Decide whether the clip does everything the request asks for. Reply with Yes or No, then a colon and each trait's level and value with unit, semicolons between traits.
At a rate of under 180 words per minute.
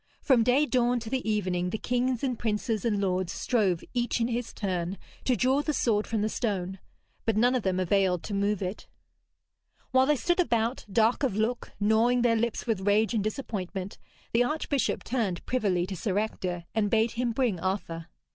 No: average, 190 wpm